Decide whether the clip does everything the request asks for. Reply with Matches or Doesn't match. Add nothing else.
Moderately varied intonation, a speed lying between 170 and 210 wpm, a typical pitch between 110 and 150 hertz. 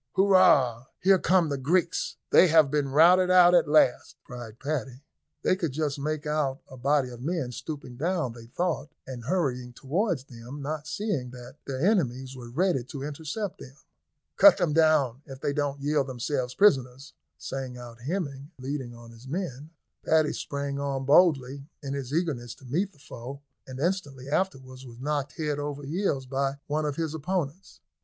Matches